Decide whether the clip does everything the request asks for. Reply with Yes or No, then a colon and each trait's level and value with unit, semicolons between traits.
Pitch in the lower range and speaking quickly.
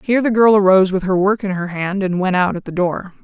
No: high, 190 Hz; fast, 295 wpm